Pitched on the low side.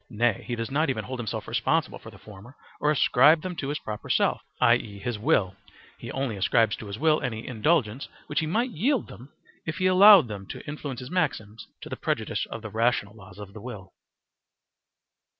Yes: low, 120 Hz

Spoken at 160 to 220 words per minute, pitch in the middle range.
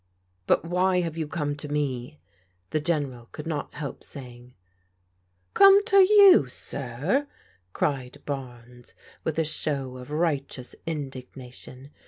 No: slow, 135 wpm; medium, 145 Hz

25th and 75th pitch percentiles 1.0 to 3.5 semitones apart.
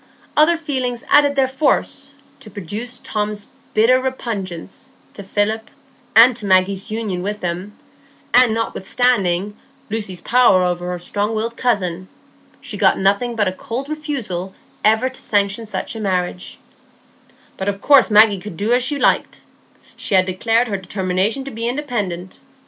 No: average, 4.5 semitones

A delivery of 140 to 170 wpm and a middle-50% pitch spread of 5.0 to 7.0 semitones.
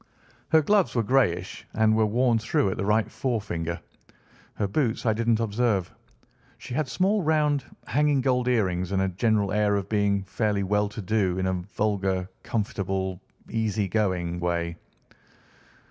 No: average, 155 wpm; average, 4.1 semitones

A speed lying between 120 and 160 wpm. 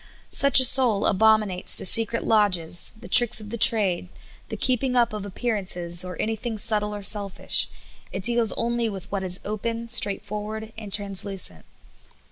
Yes: average, 155 wpm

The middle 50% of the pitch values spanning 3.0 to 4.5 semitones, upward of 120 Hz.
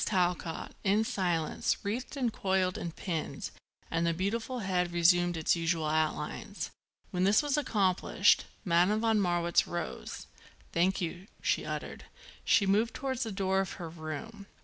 Yes: average, 3.6 semitones; medium, 185 Hz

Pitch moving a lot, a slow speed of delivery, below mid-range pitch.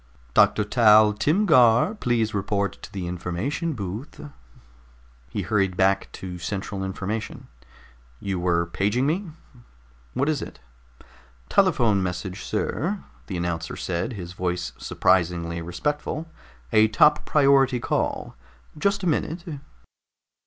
Yes: wide, 7.1 semitones; slow, 115 wpm; low, 105 Hz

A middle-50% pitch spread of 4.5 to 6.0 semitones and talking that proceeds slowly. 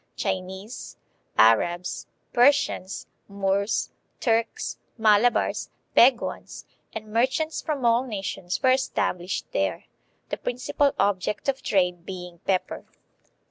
Yes: average, 5.1 semitones; slow, 100 wpm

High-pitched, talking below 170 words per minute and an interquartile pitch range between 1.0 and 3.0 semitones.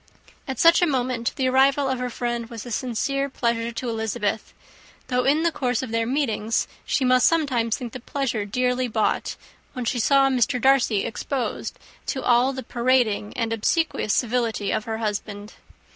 No: high, 245 Hz; average, 175 wpm; average, 2.7 semitones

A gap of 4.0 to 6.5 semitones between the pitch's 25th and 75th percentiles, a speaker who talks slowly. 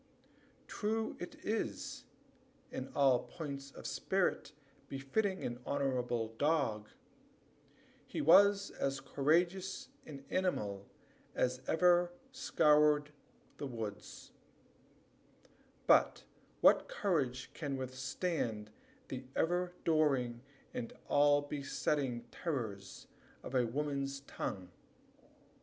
Yes: average, 4.7 semitones; slow, 90 wpm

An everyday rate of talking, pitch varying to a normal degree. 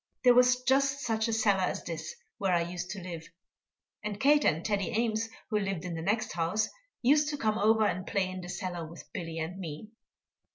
No: fast, 210 wpm; average, 4.4 semitones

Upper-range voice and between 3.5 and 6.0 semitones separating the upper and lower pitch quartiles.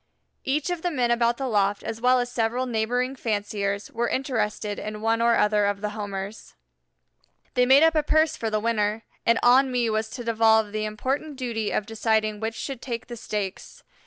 No: high, 225 Hz; average, 2.8 semitones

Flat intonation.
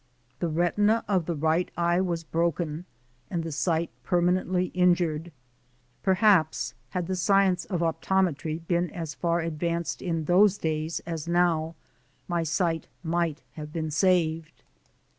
Yes: narrow, 1.9 semitones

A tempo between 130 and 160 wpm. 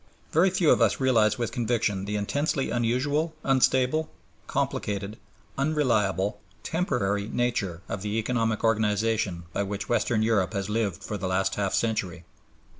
Yes: average, 140 wpm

